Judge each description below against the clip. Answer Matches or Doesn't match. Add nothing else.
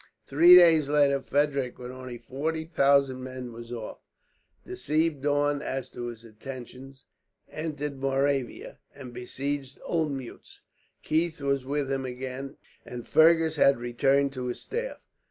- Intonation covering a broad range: Doesn't match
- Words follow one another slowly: Matches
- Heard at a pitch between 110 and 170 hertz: Matches